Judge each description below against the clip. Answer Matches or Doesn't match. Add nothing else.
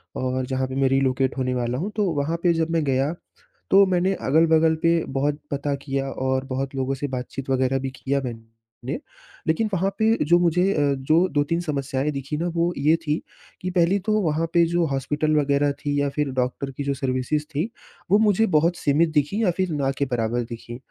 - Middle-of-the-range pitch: Matches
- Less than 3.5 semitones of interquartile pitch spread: Doesn't match